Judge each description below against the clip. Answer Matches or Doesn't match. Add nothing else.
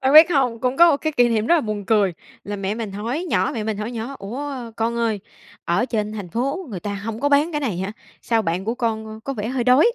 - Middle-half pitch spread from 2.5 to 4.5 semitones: Matches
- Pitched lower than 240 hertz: Matches